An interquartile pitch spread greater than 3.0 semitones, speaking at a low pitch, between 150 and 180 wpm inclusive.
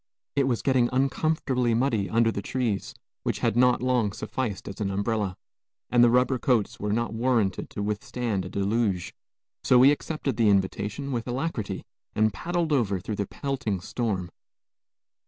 Yes: average, 3.9 semitones; low, 115 Hz; average, 160 wpm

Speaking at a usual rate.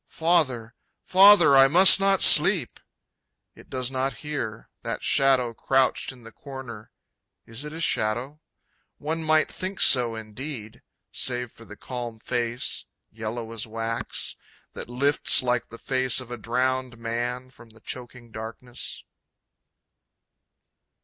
No: slow, 130 wpm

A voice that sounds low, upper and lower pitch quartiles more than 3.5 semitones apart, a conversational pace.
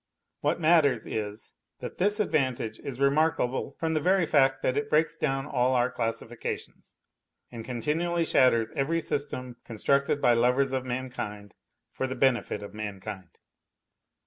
Yes: low, 130 Hz; average, 3.9 semitones; average, 145 wpm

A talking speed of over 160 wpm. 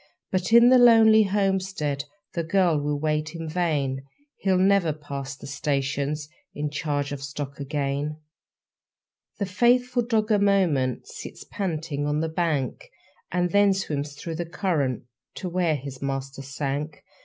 No: average, 145 wpm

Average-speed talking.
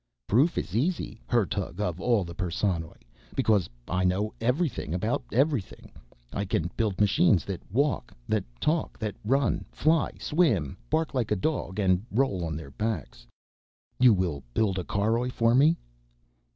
Yes: average, 150 wpm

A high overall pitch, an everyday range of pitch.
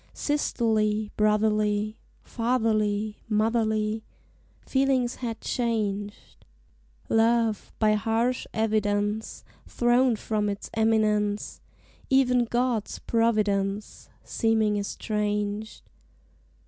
No: high, 220 Hz; narrow, 1.7 semitones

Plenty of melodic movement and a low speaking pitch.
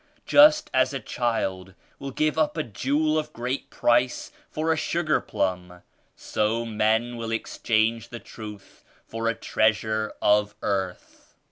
No: average, 4.4 semitones; low, 115 Hz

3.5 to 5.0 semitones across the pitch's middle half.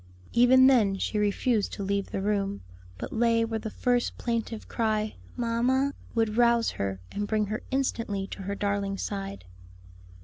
No: average, 2.8 semitones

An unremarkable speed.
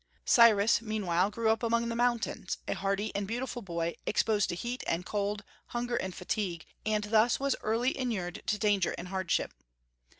Yes: average, 170 wpm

